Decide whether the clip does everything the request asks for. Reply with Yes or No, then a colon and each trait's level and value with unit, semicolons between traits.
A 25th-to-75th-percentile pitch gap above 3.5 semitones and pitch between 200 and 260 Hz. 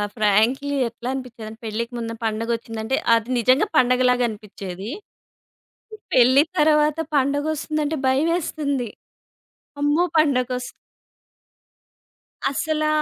Yes: average, 4.3 semitones; very high, 255 Hz